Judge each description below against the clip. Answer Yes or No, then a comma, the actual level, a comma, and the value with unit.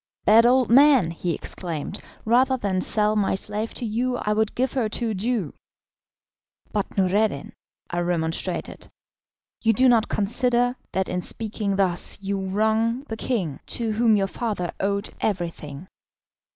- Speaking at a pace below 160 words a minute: Yes, average, 150 wpm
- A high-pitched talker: Yes, high, 210 Hz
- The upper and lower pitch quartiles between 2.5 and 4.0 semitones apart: Yes, average, 3.7 semitones